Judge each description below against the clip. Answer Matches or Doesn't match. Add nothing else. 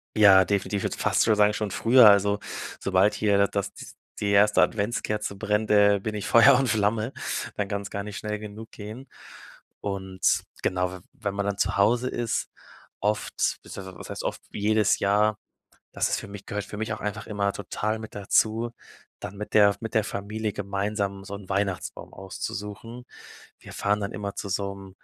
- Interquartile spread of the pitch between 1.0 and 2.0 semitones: Matches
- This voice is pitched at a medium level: Doesn't match